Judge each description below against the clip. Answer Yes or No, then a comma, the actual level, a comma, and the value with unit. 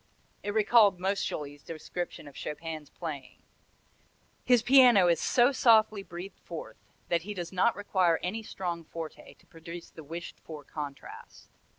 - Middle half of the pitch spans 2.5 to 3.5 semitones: No, average, 4.2 semitones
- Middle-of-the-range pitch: Yes, medium, 175 Hz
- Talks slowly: No, average, 145 wpm